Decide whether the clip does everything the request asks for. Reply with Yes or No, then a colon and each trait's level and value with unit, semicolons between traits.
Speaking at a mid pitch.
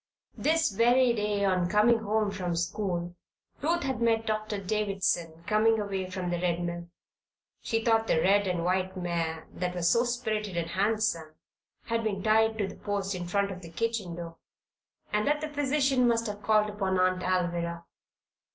No: high, 200 Hz